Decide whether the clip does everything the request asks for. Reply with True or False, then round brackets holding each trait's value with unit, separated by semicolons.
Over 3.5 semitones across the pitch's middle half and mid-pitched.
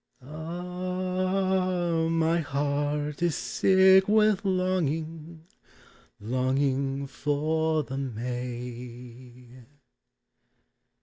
True (5.4 semitones; 155 Hz)